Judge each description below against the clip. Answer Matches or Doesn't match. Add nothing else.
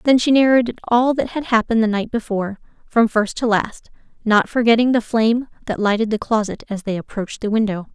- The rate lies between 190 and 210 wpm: Matches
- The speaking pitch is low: Doesn't match